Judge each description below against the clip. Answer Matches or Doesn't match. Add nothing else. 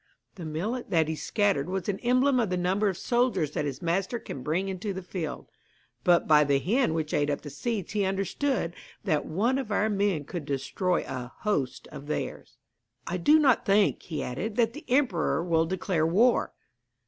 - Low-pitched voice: Doesn't match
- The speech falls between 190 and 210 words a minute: Matches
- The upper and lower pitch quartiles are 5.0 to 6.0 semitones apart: Matches